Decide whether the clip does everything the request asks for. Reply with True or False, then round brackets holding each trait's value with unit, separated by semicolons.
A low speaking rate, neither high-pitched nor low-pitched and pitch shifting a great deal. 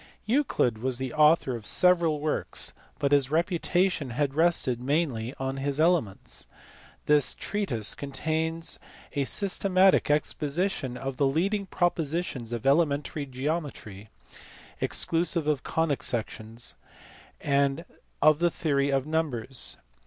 False (115 wpm; 145 Hz; 4.0 semitones)